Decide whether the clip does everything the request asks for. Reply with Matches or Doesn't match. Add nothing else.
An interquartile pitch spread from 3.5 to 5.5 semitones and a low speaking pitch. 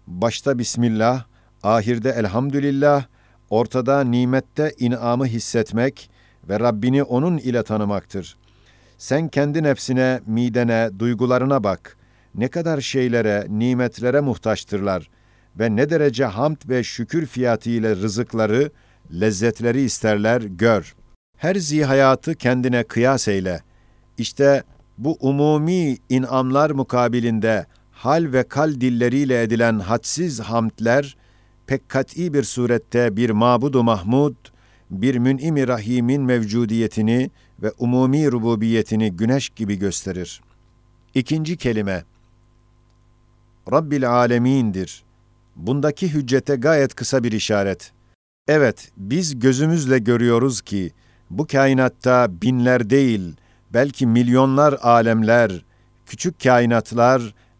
Doesn't match